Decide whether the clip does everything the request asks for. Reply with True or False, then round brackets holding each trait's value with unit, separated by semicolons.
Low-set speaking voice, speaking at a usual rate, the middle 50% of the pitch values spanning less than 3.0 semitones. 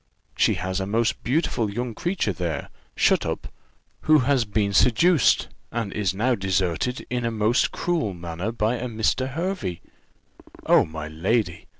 False (110 Hz; 155 wpm; 4.8 semitones)